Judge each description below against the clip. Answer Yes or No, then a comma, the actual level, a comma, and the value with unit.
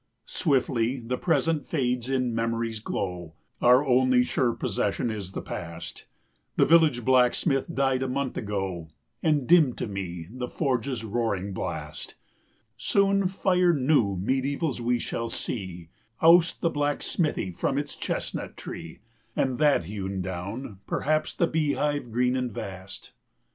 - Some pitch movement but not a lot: No, wide, 5.9 semitones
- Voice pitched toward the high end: No, low, 125 Hz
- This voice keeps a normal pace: Yes, average, 145 wpm